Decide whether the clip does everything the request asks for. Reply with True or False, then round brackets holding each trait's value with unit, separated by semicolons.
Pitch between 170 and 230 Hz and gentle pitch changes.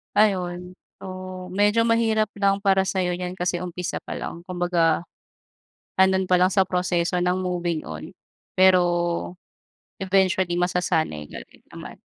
True (185 Hz; 1.3 semitones)